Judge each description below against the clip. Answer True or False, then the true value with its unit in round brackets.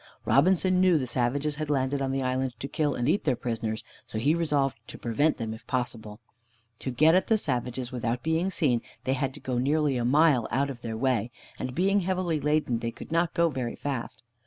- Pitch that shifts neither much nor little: True (4.3 semitones)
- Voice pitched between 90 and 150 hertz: True (135 Hz)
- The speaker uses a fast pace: True (215 wpm)